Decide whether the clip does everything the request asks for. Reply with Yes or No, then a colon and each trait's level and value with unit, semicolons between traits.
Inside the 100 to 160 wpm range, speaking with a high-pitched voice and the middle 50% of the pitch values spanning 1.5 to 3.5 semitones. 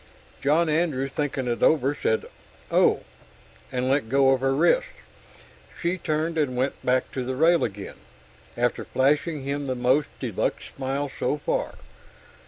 No: average, 155 wpm; medium, 140 Hz; average, 2.8 semitones